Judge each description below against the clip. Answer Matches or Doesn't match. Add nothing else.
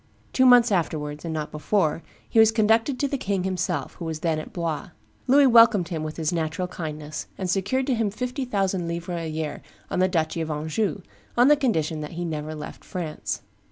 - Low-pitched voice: Doesn't match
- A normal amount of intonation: Doesn't match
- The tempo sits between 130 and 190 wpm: Doesn't match